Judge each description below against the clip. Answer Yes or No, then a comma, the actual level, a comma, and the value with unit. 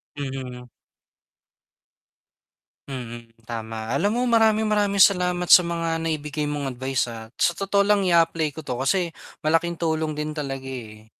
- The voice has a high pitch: No, medium, 155 Hz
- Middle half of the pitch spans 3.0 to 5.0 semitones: No, wide, 5.4 semitones